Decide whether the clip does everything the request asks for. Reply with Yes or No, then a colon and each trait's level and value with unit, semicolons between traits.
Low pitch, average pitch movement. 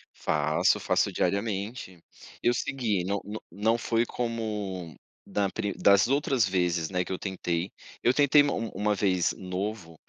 Yes: low, 100 Hz; average, 3.8 semitones